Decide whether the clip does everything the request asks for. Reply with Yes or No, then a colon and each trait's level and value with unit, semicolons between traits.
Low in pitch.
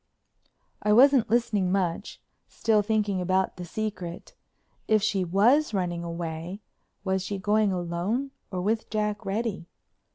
No: high, 200 Hz